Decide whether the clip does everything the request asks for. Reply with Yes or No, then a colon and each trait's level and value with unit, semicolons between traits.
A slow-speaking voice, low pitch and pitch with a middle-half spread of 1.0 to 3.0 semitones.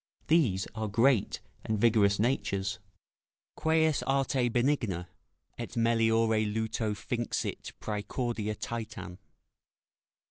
Yes: slow, 85 wpm; low, 115 Hz; narrow, 2.6 semitones